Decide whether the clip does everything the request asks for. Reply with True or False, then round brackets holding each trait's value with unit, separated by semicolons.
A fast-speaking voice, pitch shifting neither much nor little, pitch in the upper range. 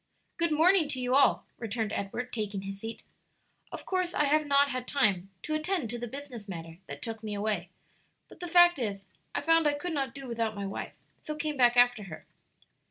False (210 wpm; 6.2 semitones; 245 Hz)